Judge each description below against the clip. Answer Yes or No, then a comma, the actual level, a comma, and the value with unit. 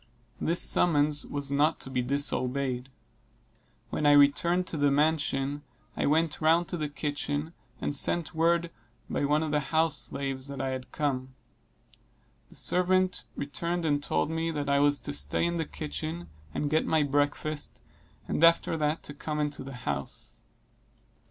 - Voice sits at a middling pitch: Yes, medium, 145 Hz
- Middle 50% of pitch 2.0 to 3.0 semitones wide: Yes, narrow, 2.5 semitones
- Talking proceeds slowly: No, average, 165 wpm